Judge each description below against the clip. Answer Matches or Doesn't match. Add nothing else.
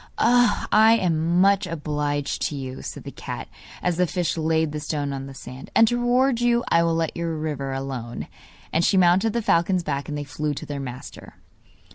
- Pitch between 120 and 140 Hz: Doesn't match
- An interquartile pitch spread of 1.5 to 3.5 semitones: Doesn't match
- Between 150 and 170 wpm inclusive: Doesn't match